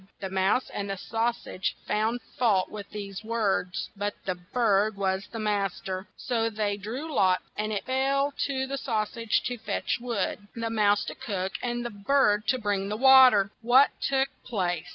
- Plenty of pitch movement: No, average, 3.6 semitones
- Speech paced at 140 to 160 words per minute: No, average, 185 wpm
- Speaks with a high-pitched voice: Yes, high, 215 Hz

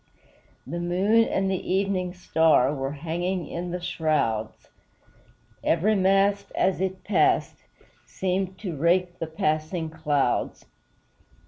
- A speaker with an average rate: No, slow, 115 wpm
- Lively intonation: No, average, 3.1 semitones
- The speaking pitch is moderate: Yes, medium, 175 Hz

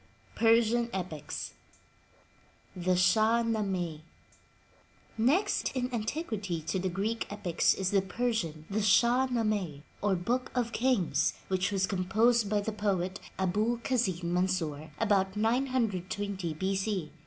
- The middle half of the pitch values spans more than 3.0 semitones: Yes, average, 3.9 semitones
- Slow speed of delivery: Yes, slow, 120 wpm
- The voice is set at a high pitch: Yes, high, 200 Hz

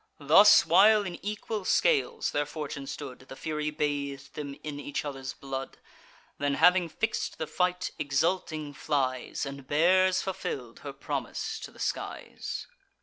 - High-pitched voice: No, medium, 150 Hz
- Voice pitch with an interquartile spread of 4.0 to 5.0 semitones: Yes, average, 4.6 semitones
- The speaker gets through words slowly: No, average, 145 wpm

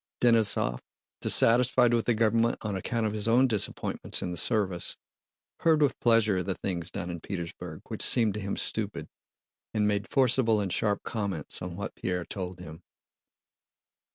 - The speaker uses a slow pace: No, average, 165 wpm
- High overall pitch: No, low, 105 Hz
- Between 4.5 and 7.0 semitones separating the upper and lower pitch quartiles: No, average, 4.1 semitones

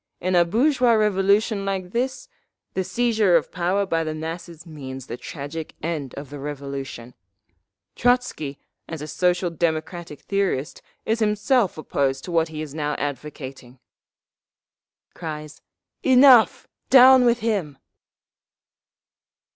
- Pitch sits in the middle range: Yes, medium, 170 Hz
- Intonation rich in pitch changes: Yes, wide, 6.0 semitones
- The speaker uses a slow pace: Yes, slow, 125 wpm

